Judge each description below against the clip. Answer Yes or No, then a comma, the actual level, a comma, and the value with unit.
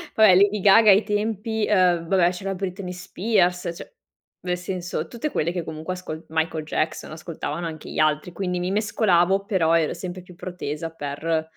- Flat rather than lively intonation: No, average, 3.1 semitones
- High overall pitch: No, medium, 180 Hz